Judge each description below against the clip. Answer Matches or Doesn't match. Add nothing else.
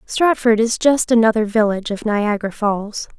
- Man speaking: Doesn't match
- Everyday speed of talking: Matches